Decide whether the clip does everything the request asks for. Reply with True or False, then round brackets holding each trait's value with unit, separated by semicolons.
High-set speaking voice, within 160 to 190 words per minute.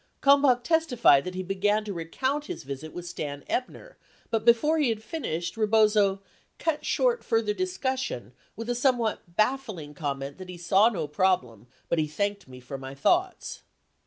True (205 Hz; 170 wpm)